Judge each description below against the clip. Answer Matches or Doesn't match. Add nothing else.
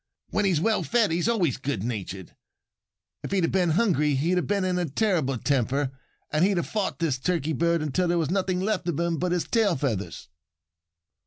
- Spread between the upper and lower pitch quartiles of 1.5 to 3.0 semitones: Doesn't match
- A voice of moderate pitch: Matches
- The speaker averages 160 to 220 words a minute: Matches